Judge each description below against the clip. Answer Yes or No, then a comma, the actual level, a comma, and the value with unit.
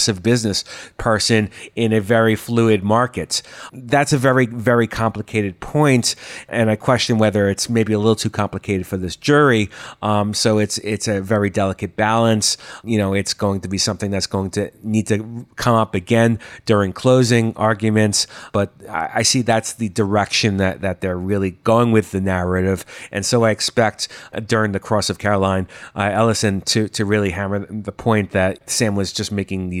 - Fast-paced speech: No, average, 185 wpm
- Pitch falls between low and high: No, low, 110 Hz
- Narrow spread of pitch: Yes, narrow, 2.3 semitones